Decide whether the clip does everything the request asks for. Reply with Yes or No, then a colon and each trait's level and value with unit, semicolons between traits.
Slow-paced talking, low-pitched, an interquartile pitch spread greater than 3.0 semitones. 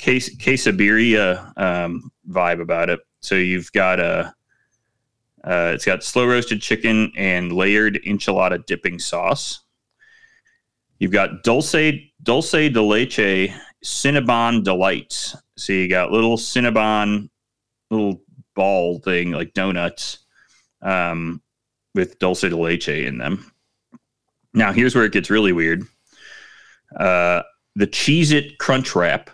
Yes: slow, 120 wpm; low, 105 Hz; average, 5.0 semitones